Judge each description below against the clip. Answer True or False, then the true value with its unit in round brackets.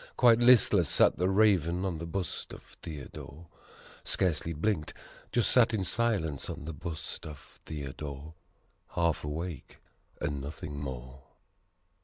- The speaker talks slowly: True (130 wpm)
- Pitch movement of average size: True (4.6 semitones)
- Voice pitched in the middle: False (80 Hz)